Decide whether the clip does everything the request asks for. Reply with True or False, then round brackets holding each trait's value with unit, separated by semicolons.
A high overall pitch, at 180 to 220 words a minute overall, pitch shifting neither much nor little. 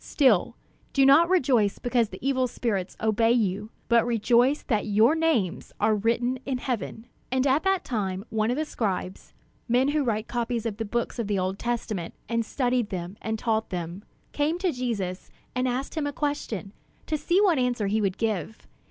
True (235 Hz; 185 wpm; 3.8 semitones)